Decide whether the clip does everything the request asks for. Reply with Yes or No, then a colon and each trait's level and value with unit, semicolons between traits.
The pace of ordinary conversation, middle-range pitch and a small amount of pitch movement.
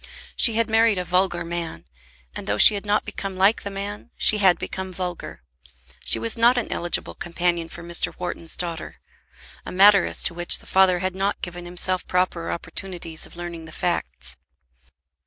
Yes: average, 180 wpm; medium, 180 Hz; narrow, 2.3 semitones